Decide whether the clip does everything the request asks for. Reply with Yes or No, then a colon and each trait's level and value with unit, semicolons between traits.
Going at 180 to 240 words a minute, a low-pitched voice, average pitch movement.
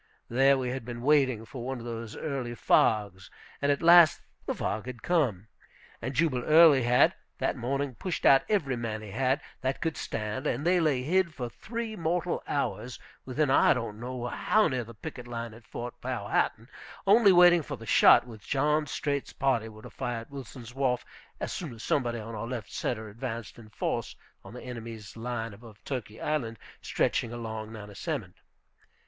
Yes: average, 185 wpm; low, 125 Hz; average, 3.9 semitones